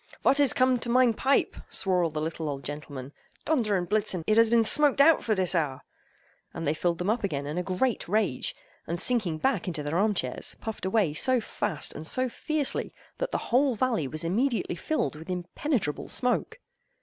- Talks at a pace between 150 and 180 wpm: No, average, 195 wpm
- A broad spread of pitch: Yes, wide, 7.6 semitones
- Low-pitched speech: No, high, 200 Hz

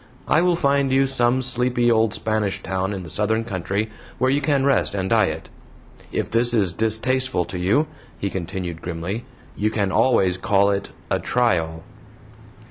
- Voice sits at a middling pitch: No, low, 110 Hz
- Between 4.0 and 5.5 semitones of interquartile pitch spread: Yes, average, 4.8 semitones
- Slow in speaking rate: No, average, 165 wpm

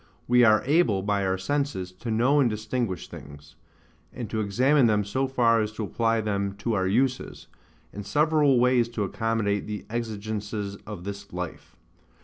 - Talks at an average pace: Yes, average, 165 wpm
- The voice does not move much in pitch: No, average, 3.5 semitones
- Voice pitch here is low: Yes, low, 110 Hz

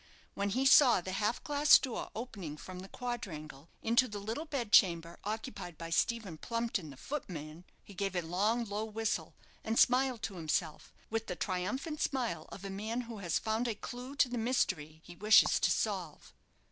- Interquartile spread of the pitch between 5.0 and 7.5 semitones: Yes, average, 5.3 semitones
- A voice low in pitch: No, high, 210 Hz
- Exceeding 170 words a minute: Yes, average, 180 wpm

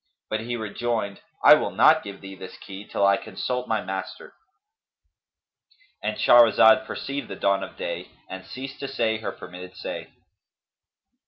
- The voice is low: Yes, low, 110 Hz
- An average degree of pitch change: Yes, average, 4.4 semitones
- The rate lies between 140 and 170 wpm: Yes, average, 150 wpm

